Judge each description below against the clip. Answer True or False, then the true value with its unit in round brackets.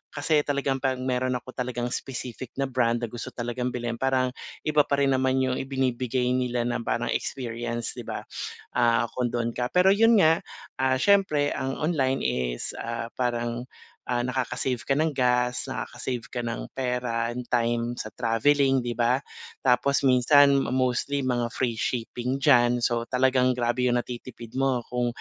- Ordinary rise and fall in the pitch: False (1.8 semitones)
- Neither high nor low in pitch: False (125 Hz)